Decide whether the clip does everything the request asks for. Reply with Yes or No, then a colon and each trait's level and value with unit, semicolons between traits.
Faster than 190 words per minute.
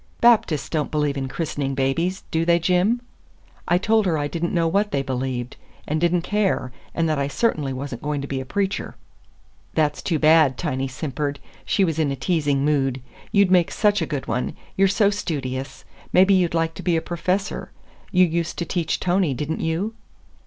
Yes: average, 200 wpm